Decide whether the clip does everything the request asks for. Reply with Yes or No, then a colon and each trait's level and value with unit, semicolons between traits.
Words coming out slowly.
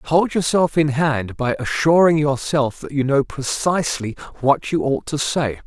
No: average, 170 wpm